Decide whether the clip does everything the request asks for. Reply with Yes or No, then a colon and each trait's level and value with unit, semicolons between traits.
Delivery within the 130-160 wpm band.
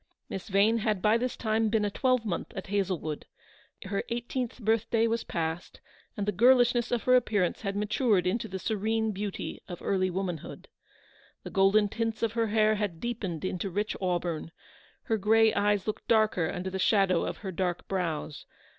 No: average, 175 wpm